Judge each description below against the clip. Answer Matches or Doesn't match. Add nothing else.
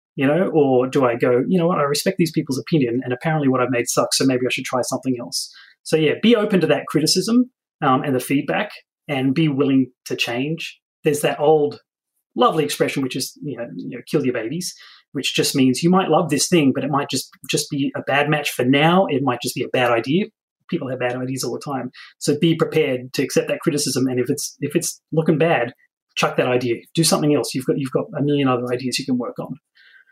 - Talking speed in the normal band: Doesn't match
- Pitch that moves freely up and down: Doesn't match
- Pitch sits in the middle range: Matches